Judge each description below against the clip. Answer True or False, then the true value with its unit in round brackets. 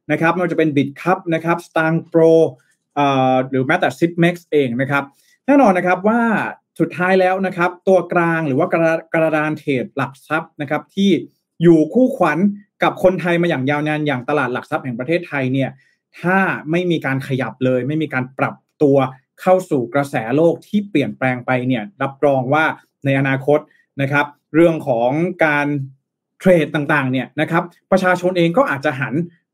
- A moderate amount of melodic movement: True (3.9 semitones)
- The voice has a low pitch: False (155 Hz)